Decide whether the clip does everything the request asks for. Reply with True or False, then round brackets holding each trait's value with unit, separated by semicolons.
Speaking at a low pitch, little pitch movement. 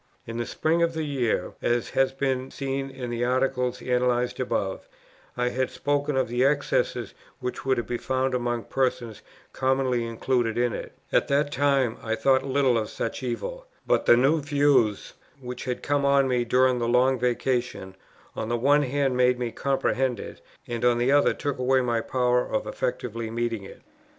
True (125 Hz; 2.2 semitones)